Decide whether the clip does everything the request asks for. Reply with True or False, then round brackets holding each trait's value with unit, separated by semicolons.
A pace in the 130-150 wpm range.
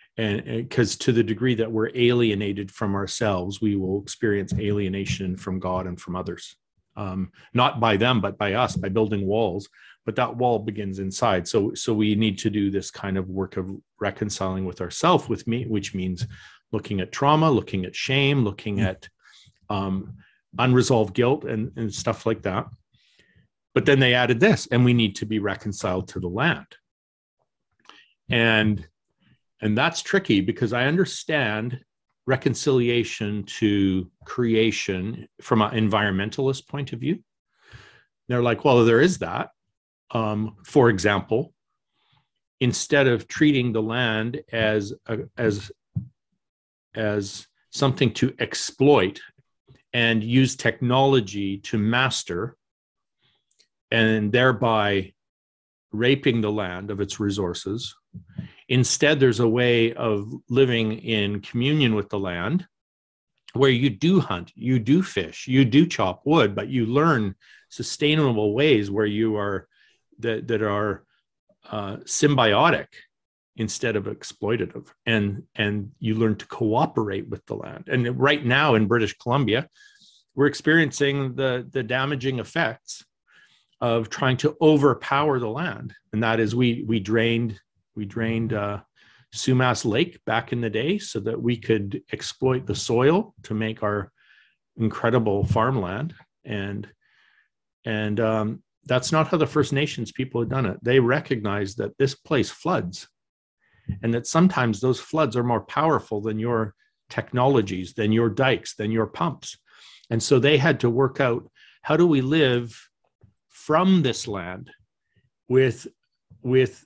True (140 wpm)